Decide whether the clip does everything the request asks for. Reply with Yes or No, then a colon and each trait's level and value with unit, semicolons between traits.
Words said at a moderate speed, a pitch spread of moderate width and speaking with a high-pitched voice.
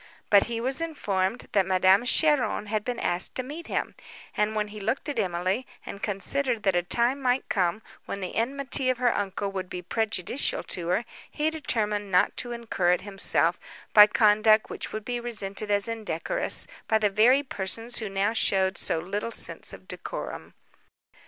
Yes: average, 180 wpm; average, 4.0 semitones; high, 215 Hz